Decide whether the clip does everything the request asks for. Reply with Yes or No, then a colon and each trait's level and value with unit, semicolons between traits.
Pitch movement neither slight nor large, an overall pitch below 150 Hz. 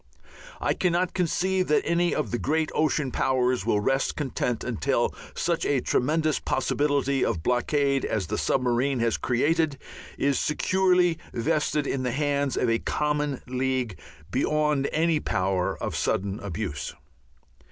Yes: average, 3.7 semitones; medium, 140 Hz